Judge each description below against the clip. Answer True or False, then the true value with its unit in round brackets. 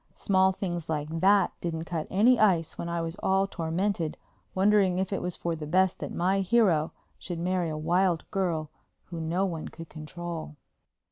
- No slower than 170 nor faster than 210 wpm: True (180 wpm)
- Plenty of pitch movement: False (2.7 semitones)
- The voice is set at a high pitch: False (175 Hz)